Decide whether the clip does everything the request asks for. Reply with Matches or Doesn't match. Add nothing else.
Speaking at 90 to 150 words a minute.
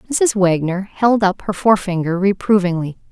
Matches